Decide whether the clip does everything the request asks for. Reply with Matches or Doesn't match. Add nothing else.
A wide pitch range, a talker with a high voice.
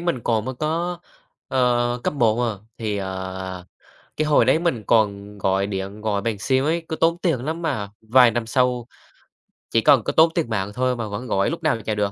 Doesn't match